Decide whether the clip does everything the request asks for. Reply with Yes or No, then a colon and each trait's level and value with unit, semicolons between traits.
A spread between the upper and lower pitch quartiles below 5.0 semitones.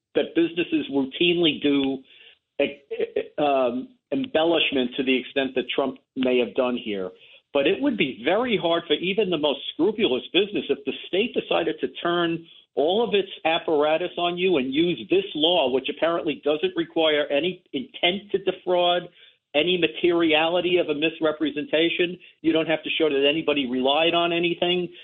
Yes: average, 3.9 semitones